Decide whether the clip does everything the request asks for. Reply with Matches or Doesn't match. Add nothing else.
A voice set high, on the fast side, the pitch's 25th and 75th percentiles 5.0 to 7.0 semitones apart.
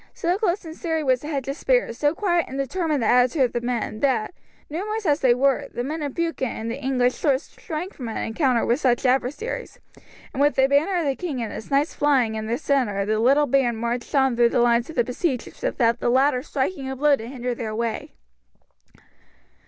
Doesn't match